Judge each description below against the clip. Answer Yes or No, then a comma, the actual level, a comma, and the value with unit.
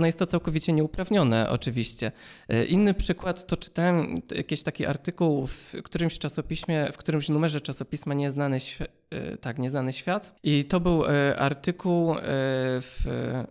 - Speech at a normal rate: Yes, average, 135 wpm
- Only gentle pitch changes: No, average, 4.4 semitones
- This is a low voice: No, medium, 155 Hz